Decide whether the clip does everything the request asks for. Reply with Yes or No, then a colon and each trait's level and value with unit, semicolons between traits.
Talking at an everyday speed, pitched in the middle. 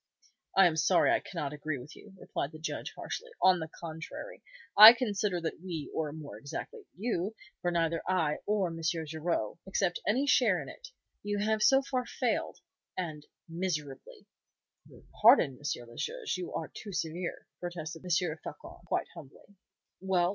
Yes: average, 165 wpm; medium, 175 Hz